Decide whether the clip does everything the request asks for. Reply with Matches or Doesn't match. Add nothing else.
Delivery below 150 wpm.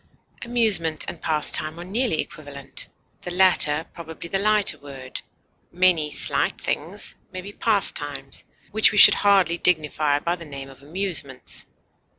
Matches